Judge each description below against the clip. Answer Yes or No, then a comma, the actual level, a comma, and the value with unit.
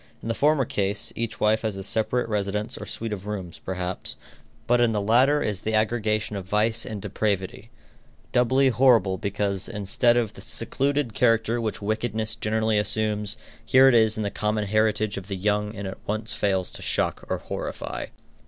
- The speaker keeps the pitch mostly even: Yes, narrow, 2.1 semitones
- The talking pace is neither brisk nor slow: Yes, average, 180 wpm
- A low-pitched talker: Yes, low, 110 Hz